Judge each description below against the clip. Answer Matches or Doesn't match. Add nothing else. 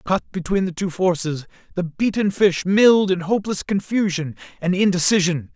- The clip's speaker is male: Matches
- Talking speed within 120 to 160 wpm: Matches